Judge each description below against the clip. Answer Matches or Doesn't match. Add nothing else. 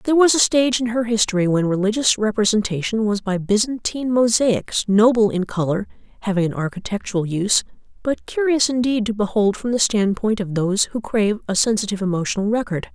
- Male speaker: Doesn't match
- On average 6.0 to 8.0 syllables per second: Matches